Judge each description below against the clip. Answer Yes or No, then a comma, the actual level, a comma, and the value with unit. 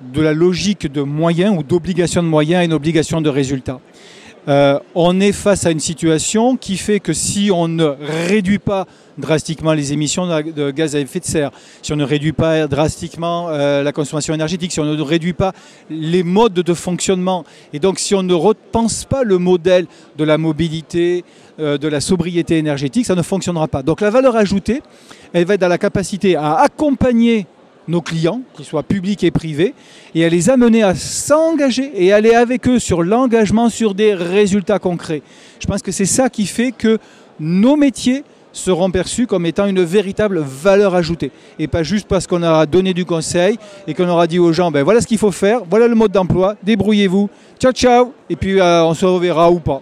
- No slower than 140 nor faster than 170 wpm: No, average, 200 wpm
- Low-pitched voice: No, medium, 180 Hz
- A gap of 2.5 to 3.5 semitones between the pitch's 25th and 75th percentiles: No, average, 4.5 semitones